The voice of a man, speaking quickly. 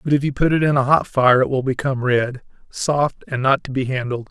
Yes: male; fast, 265 wpm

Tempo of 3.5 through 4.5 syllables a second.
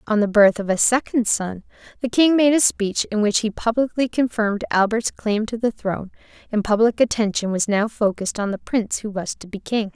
No: 5.5 syllables/s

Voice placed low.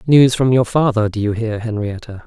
Yes: low, 115 Hz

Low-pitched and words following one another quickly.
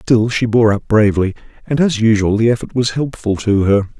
Yes: low, 115 Hz; fast, 210 wpm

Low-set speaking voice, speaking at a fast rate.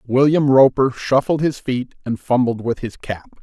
No: low, 130 Hz; average, 175 wpm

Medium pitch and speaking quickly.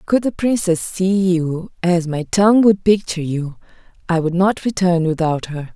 No: medium, 180 Hz; average, 175 wpm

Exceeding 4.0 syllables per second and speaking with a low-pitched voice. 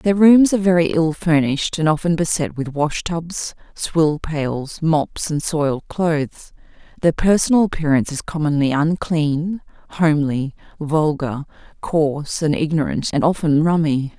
No: 4.5 syllables/s; medium, 155 Hz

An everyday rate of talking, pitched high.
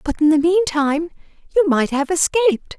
Yes: average, 170 wpm; very high, 325 Hz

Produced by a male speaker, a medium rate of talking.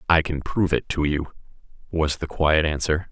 Yes: male; average, 195 wpm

